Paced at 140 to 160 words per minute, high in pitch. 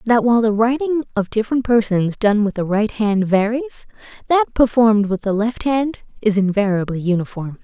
No: average, 175 wpm; high, 220 Hz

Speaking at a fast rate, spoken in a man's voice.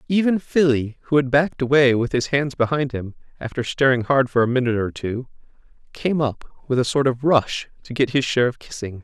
Yes: fast, 215 wpm; male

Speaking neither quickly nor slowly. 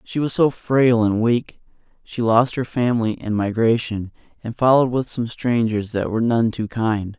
Yes: average, 185 wpm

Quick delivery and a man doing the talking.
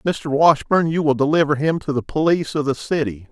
Yes: fast, 215 wpm; male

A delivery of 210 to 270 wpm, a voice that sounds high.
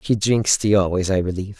No: fast, 225 wpm; low, 100 Hz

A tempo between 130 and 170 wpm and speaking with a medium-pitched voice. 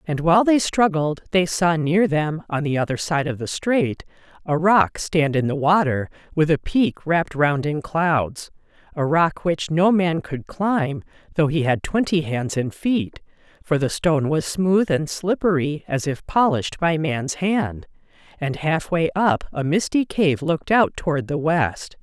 No: average, 180 wpm; medium, 160 Hz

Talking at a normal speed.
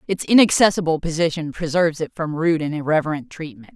Yes: average, 160 wpm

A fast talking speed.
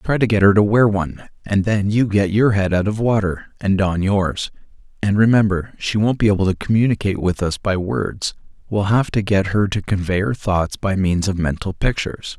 Yes: fast, 215 wpm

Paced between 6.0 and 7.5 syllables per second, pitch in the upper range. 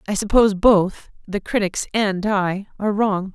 No: 4.6 syllables/s; high, 200 Hz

